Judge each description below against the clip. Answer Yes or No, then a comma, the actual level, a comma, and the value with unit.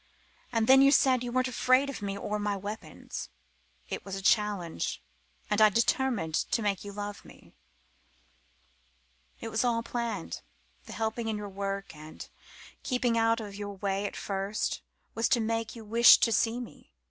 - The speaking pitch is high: Yes, high, 215 Hz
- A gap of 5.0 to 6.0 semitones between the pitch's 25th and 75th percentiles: No, average, 2.7 semitones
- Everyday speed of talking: Yes, average, 170 wpm